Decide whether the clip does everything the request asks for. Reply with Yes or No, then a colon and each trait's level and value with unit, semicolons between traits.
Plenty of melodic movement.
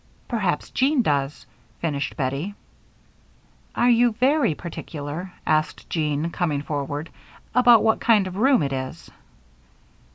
Yes: wide, 8.0 semitones